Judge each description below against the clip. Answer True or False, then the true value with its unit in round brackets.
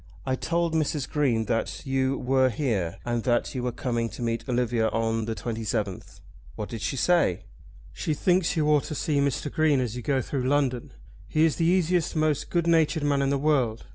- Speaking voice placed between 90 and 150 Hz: True (135 Hz)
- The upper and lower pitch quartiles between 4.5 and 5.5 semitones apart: True (4.8 semitones)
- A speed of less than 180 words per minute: False (200 wpm)